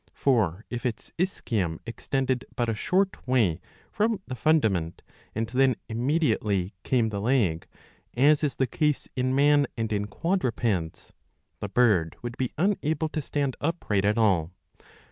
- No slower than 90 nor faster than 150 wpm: Yes, average, 145 wpm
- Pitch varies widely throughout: Yes, wide, 5.7 semitones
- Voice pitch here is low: Yes, low, 120 Hz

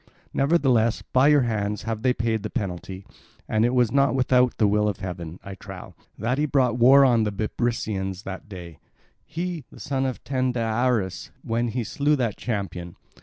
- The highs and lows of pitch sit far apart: No, average, 4.1 semitones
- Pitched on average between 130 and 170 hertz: No, low, 115 Hz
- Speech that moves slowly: No, average, 170 wpm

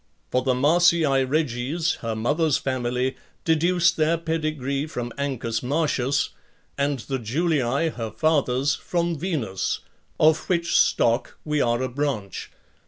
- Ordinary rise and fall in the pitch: Yes, average, 4.4 semitones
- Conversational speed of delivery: No, slow, 125 wpm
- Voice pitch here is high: No, medium, 140 Hz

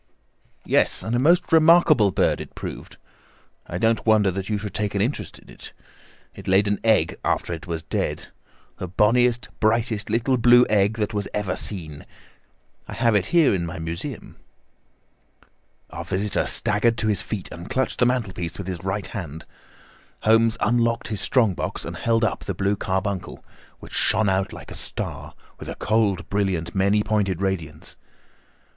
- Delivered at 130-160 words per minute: No, average, 170 wpm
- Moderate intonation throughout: Yes, average, 3.2 semitones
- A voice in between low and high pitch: No, low, 105 Hz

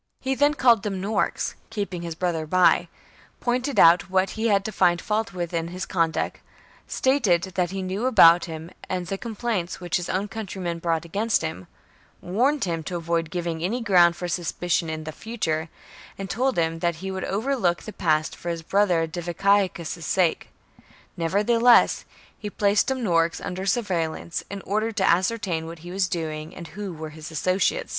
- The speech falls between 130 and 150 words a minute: No, average, 180 wpm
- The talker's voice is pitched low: No, medium, 185 Hz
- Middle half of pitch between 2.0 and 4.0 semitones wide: Yes, average, 3.7 semitones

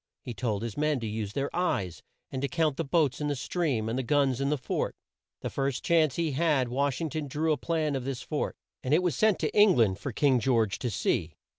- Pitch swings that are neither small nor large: Yes, average, 4.3 semitones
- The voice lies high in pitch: No, medium, 140 Hz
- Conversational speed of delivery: No, fast, 250 wpm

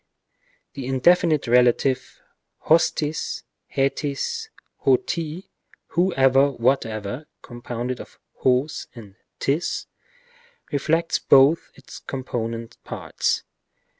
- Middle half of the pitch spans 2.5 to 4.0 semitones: Yes, average, 3.7 semitones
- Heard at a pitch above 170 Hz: No, low, 135 Hz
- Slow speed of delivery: Yes, slow, 85 wpm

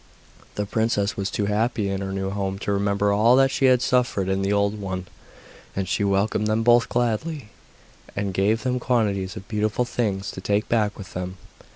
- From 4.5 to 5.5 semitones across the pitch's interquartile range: No, average, 2.7 semitones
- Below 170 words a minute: No, average, 195 wpm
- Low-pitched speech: Yes, low, 105 Hz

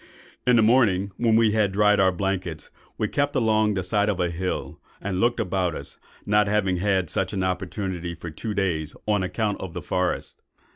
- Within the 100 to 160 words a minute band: No, average, 195 wpm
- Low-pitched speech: Yes, low, 100 Hz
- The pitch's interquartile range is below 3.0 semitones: Yes, narrow, 2.6 semitones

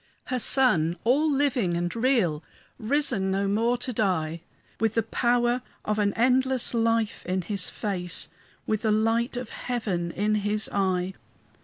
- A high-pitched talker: Yes, high, 220 Hz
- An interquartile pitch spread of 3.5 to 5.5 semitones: Yes, average, 4.3 semitones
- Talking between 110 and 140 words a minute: No, average, 150 wpm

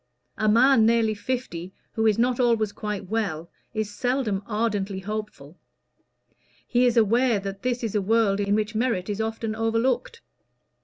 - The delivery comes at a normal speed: Yes, average, 155 wpm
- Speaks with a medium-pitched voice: No, high, 220 Hz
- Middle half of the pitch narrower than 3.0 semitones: Yes, narrow, 2.4 semitones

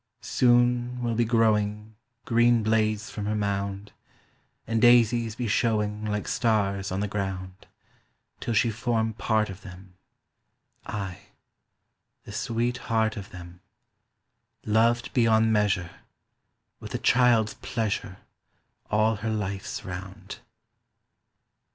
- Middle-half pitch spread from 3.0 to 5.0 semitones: No, narrow, 2.4 semitones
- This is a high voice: No, low, 110 Hz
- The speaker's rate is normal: No, slow, 110 wpm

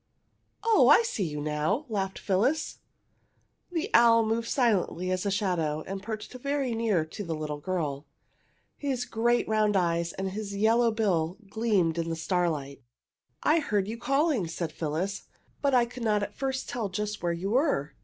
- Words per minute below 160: No, average, 170 wpm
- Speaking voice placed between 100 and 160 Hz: No, high, 205 Hz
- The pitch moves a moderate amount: No, wide, 5.7 semitones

